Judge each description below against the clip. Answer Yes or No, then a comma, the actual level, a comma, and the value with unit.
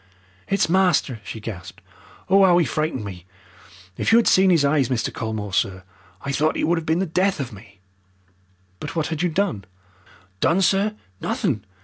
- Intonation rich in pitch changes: Yes, wide, 9.0 semitones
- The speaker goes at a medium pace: Yes, average, 180 wpm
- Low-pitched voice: No, medium, 155 Hz